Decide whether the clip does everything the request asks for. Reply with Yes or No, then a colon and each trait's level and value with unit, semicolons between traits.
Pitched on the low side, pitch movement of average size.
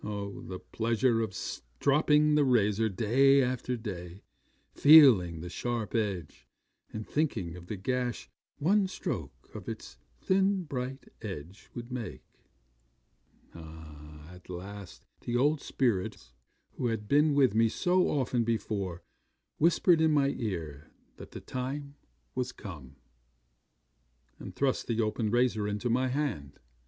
No: low, 115 Hz; wide, 6.2 semitones